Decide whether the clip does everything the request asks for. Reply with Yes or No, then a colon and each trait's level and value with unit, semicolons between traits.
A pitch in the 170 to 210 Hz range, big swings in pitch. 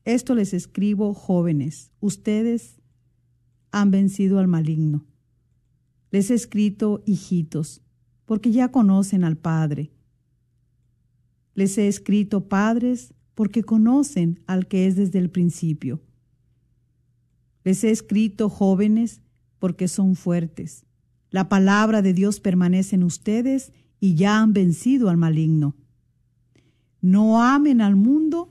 Yes: medium, 185 Hz; wide, 8.3 semitones